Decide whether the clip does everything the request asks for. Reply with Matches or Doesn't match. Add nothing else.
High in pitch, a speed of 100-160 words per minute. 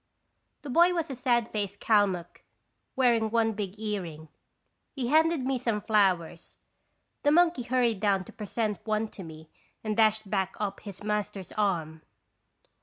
Matches